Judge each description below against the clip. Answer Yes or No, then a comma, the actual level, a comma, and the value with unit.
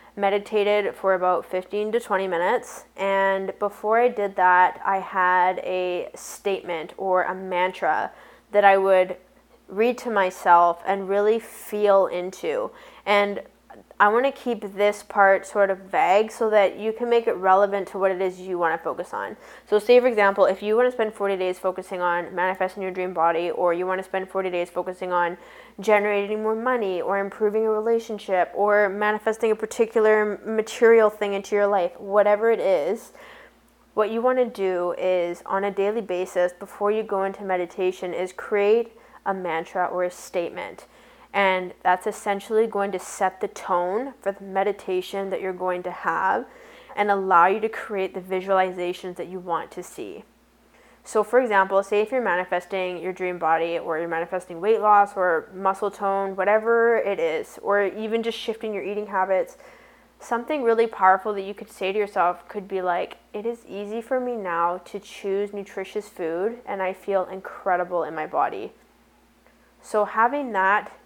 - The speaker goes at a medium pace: Yes, average, 175 wpm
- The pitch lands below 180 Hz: No, high, 195 Hz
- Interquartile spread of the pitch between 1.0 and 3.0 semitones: Yes, average, 2.7 semitones